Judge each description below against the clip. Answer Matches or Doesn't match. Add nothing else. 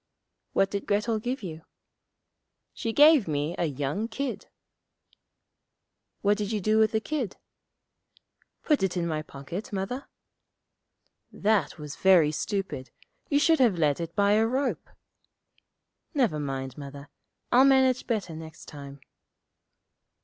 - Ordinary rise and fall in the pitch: Doesn't match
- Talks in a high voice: Matches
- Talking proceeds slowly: Matches